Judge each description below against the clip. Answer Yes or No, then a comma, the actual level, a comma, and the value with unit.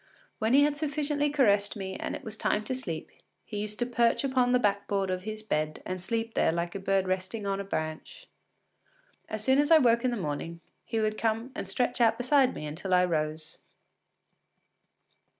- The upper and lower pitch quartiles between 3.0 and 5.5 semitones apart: Yes, average, 5.0 semitones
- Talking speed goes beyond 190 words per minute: Yes, average, 200 wpm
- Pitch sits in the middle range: No, high, 215 Hz